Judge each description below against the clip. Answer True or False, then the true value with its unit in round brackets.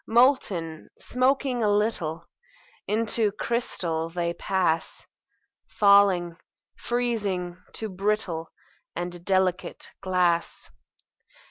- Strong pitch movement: False (4.2 semitones)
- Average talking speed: False (80 wpm)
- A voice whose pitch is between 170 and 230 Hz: True (190 Hz)